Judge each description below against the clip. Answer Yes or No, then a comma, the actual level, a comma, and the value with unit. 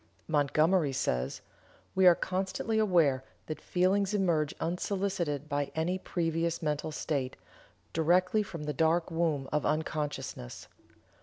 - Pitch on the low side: No, medium, 165 Hz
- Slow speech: Yes, slow, 120 wpm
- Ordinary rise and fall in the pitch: Yes, average, 3.6 semitones